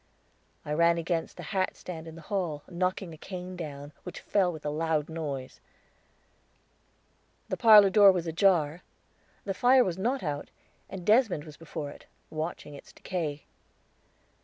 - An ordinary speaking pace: Yes, average, 150 wpm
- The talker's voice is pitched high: No, medium, 170 Hz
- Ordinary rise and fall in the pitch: Yes, average, 3.6 semitones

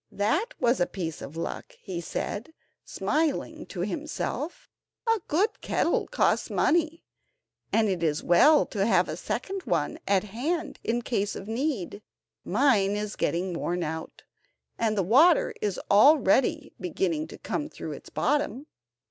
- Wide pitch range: Yes, wide, 8.6 semitones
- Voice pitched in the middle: No, high, 215 Hz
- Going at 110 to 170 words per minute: Yes, average, 150 wpm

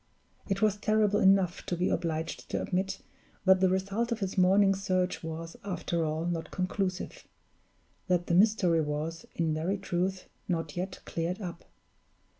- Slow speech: No, average, 155 wpm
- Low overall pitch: No, medium, 185 Hz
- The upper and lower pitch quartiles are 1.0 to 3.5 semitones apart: Yes, narrow, 2.6 semitones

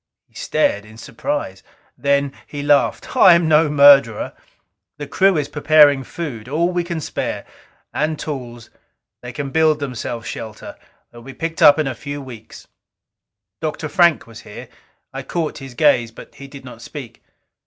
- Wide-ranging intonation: No, average, 4.3 semitones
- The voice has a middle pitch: Yes, medium, 145 Hz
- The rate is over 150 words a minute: Yes, average, 165 wpm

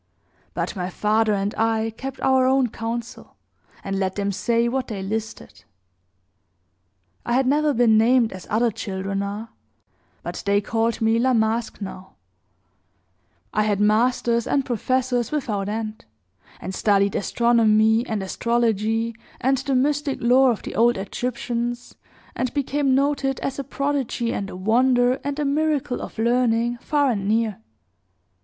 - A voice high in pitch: Yes, high, 235 Hz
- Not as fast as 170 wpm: Yes, average, 145 wpm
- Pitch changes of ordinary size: Yes, average, 3.2 semitones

